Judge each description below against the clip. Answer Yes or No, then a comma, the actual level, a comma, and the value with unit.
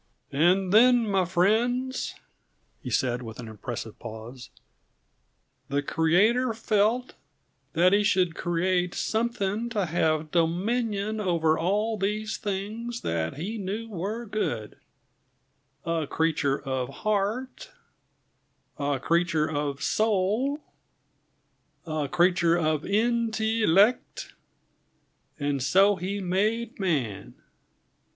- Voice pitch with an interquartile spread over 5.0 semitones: Yes, wide, 5.6 semitones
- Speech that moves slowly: Yes, slow, 105 wpm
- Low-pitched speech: No, high, 190 Hz